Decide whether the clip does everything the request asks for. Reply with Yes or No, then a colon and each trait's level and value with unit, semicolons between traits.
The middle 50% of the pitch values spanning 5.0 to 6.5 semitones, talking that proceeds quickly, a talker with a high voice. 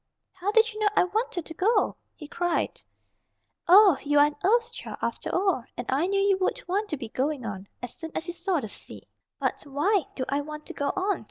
Yes: wide, 5.6 semitones; fast, 230 wpm; very high, 350 Hz